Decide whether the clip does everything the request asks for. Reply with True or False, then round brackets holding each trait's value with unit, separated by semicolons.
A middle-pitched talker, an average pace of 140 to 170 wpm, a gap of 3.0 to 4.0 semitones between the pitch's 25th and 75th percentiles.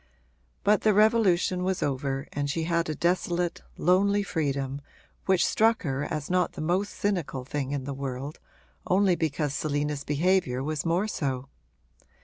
False (160 Hz; 150 wpm; 4.7 semitones)